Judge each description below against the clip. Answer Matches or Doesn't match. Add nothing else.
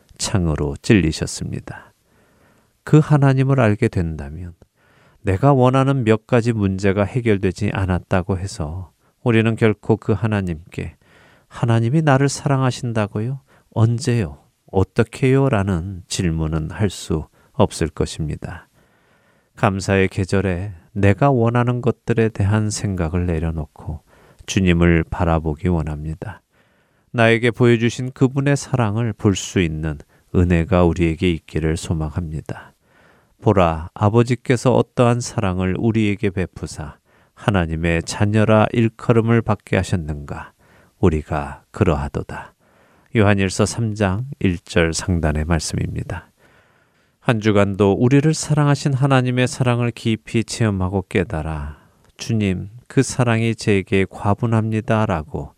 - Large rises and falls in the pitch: Doesn't match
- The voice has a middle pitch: Doesn't match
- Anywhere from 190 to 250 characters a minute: Doesn't match